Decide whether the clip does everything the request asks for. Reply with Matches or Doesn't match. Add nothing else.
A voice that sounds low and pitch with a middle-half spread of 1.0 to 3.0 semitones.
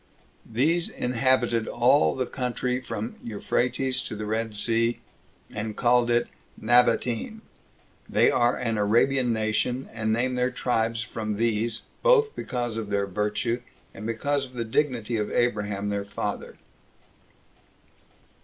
Matches